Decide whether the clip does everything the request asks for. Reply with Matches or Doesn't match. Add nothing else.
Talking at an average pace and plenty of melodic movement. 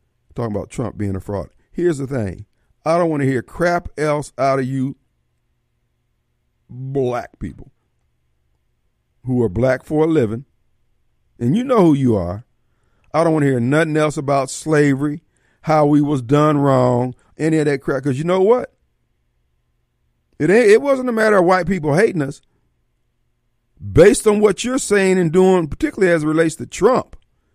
Matches